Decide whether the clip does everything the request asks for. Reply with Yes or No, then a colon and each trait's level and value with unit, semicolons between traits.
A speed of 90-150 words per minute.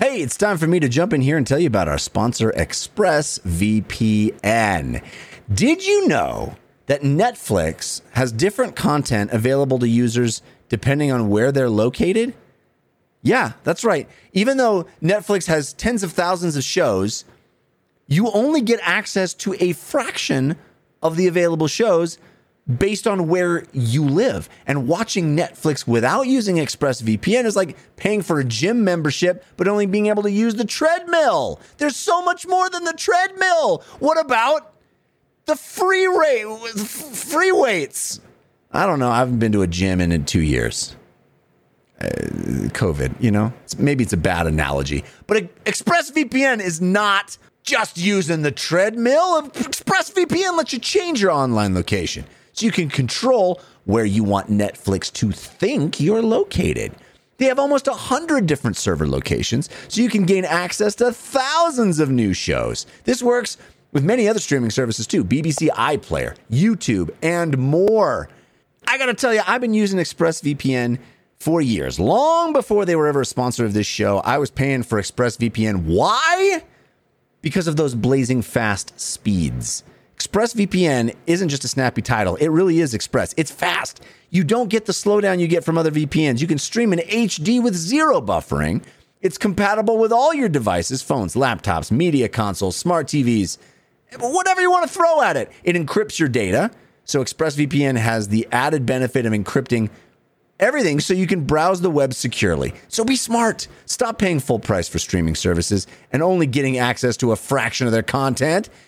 No: average, 165 wpm